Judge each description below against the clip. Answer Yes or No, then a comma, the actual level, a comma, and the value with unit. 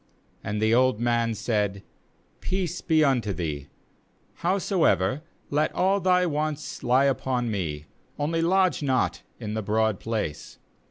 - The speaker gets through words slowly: Yes, slow, 130 wpm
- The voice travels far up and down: Yes, wide, 6.9 semitones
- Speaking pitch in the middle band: No, low, 125 Hz